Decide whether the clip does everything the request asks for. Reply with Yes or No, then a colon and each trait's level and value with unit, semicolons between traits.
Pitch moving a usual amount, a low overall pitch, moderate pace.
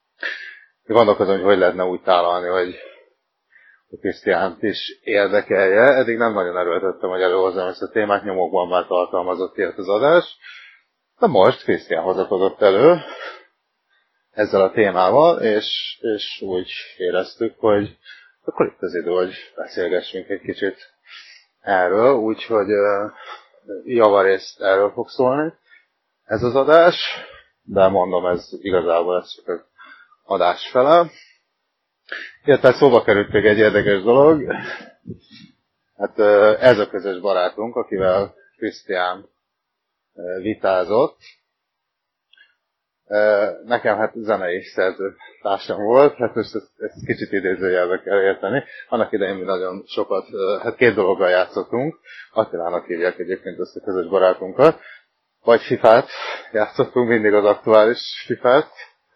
No: wide, 6.0 semitones; low, 105 Hz; average, 115 wpm